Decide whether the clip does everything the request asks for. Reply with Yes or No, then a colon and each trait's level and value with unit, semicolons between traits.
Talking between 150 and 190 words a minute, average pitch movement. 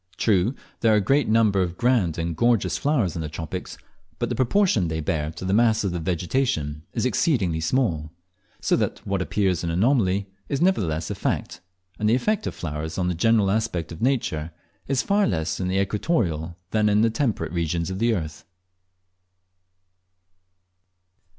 No: average, 175 wpm; wide, 5.7 semitones